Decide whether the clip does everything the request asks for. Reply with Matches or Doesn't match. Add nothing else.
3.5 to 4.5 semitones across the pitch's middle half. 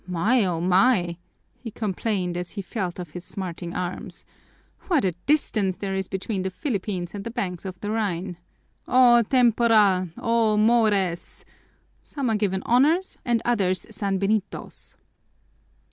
Matches